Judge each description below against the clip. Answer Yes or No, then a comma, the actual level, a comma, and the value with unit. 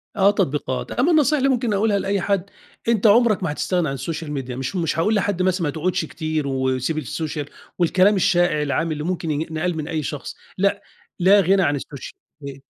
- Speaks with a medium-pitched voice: Yes, medium, 175 Hz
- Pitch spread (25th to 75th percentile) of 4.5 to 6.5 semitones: Yes, average, 5.0 semitones